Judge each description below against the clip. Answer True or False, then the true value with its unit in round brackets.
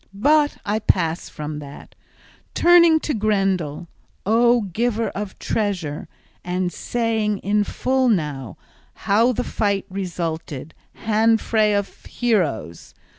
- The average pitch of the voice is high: True (205 Hz)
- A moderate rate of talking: False (110 wpm)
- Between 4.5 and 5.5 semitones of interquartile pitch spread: True (5.0 semitones)